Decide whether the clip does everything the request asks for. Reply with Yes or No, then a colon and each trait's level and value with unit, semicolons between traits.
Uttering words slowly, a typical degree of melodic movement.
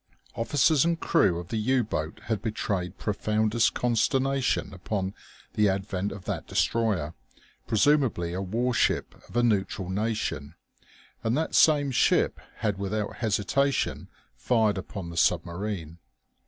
Yes: slow, 130 wpm; average, 4.3 semitones